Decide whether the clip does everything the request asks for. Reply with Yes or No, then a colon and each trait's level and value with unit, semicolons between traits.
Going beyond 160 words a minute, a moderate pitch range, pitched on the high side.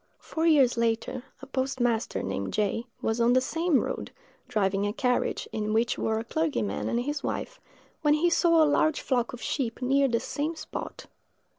Yes: average, 180 wpm; average, 4.8 semitones; very high, 255 Hz